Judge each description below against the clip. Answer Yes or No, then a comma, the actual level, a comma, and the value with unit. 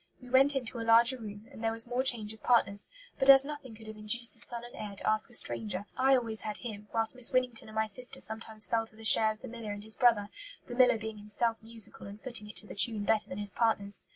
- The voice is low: No, high, 225 Hz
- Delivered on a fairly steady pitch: Yes, narrow, 2.2 semitones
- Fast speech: Yes, fast, 265 wpm